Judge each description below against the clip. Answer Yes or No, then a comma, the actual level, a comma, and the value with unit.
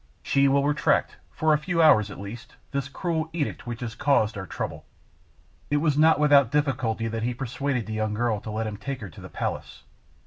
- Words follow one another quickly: Yes, fast, 210 wpm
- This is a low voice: Yes, low, 130 Hz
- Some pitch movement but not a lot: Yes, average, 4.8 semitones